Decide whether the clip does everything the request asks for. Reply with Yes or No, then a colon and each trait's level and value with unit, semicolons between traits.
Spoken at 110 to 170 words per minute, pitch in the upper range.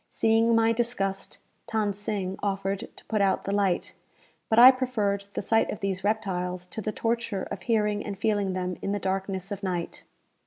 No: average, 185 wpm; high, 200 Hz